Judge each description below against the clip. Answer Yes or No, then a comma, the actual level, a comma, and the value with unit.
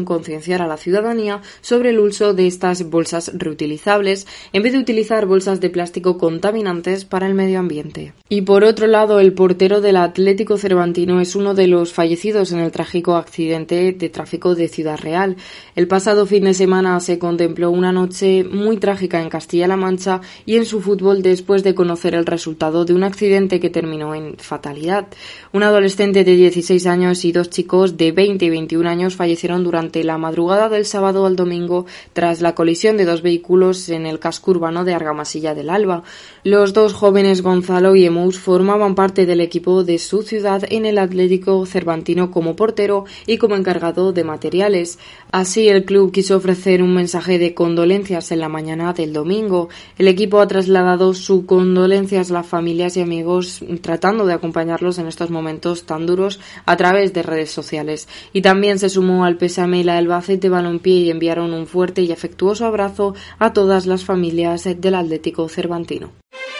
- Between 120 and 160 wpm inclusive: No, average, 180 wpm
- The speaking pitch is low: No, medium, 180 Hz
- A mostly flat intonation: Yes, narrow, 2.3 semitones